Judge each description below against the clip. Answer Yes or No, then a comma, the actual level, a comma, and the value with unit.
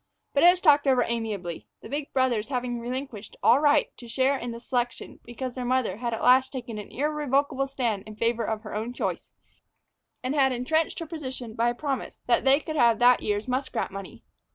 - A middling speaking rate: No, fast, 210 wpm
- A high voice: Yes, very high, 250 Hz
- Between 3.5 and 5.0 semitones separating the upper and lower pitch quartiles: No, average, 2.9 semitones